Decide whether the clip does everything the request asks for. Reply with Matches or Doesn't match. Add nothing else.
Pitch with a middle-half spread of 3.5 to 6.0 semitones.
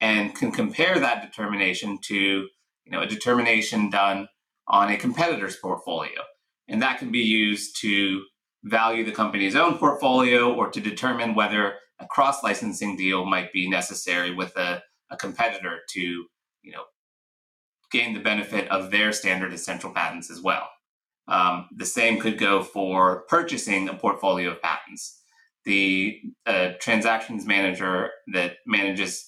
Doesn't match